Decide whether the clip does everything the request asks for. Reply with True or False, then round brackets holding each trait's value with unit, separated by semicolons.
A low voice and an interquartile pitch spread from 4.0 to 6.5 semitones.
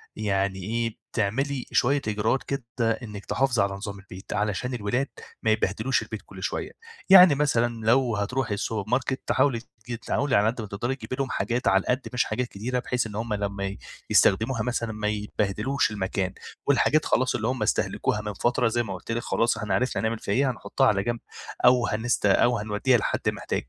False (115 Hz; 3.4 semitones)